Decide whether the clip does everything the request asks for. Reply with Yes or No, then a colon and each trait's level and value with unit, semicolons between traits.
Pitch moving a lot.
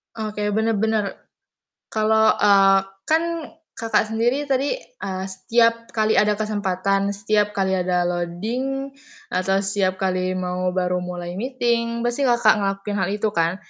No: average, 3.2 semitones